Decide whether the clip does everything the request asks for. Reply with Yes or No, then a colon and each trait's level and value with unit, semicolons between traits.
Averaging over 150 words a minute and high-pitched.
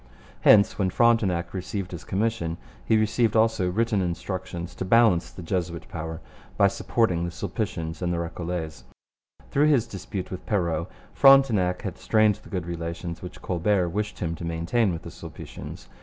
No: average, 160 wpm; very low, 90 Hz